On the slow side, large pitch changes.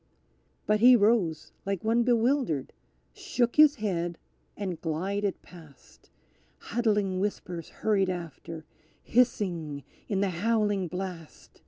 No: slow, 115 wpm; average, 4.8 semitones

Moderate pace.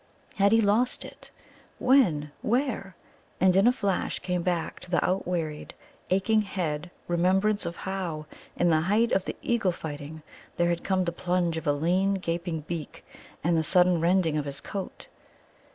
Yes: average, 170 wpm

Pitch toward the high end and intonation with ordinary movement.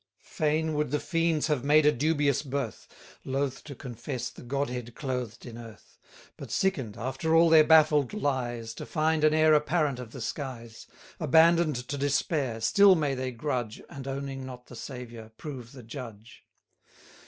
No: medium, 140 Hz; average, 4.0 semitones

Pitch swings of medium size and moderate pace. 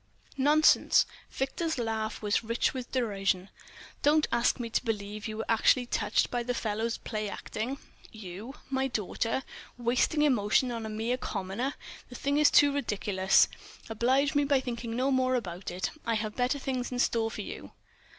Yes: average, 3.5 semitones; average, 160 wpm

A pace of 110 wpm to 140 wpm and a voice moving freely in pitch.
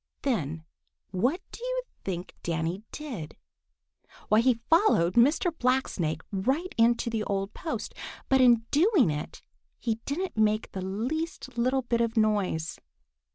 Yes: slow, 135 wpm; wide, 6.1 semitones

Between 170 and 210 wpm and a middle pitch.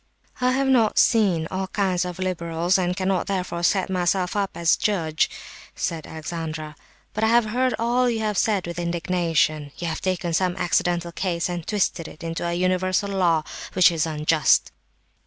Yes: average, 175 wpm; medium, 180 Hz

